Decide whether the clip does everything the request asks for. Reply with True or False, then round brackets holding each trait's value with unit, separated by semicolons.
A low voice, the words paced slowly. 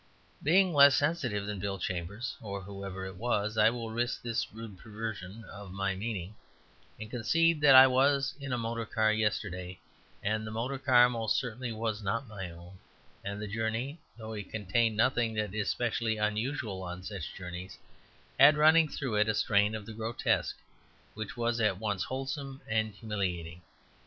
False (110 Hz; 170 wpm)